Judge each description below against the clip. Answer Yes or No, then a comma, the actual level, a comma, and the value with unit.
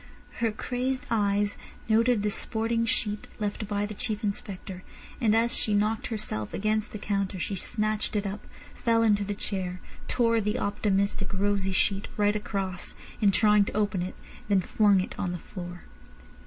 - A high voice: Yes, high, 205 Hz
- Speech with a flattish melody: Yes, narrow, 1.7 semitones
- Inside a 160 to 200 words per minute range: Yes, average, 170 wpm